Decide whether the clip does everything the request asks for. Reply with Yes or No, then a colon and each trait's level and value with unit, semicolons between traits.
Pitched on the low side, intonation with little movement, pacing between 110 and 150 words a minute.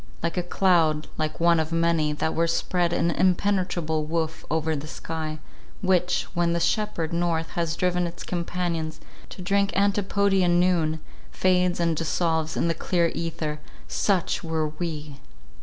No: medium, 170 Hz; narrow, 2.1 semitones; average, 145 wpm